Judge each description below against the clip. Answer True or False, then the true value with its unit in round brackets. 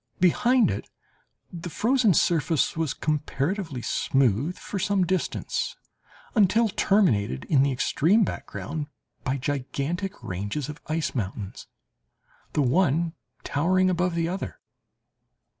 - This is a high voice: False (165 Hz)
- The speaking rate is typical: False (110 wpm)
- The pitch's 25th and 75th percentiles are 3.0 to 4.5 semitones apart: False (5.3 semitones)